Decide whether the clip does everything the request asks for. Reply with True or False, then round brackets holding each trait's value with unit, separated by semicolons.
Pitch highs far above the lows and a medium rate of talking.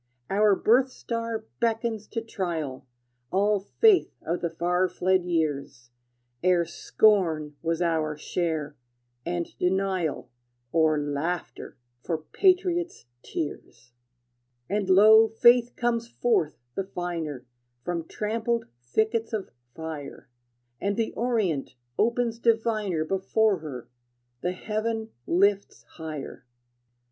False (5.7 semitones; 105 wpm)